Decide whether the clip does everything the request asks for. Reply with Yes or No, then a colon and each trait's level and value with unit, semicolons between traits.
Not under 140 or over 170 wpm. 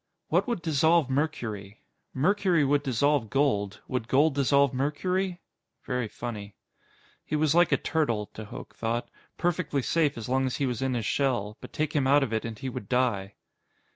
No: average, 180 wpm